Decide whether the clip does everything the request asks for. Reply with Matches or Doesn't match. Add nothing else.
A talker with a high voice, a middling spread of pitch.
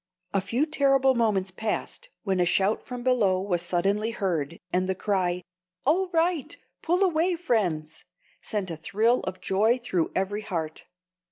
Doesn't match